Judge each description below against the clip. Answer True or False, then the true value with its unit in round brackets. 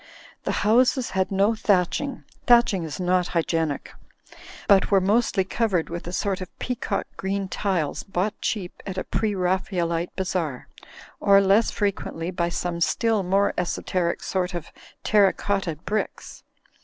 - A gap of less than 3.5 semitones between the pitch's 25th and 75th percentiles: True (2.6 semitones)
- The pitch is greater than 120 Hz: True (190 Hz)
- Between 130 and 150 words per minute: True (140 wpm)